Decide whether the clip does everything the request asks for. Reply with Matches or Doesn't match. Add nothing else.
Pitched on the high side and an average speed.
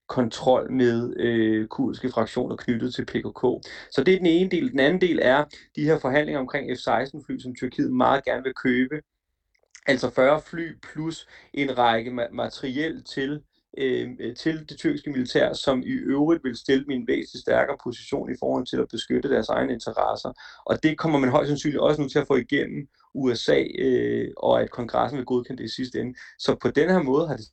Doesn't match